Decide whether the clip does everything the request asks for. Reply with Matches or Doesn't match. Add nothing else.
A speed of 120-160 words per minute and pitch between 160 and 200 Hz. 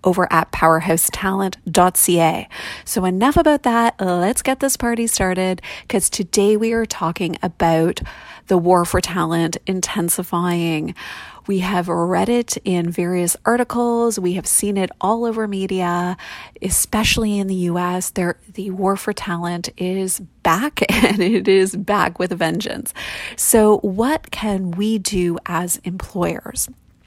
Matches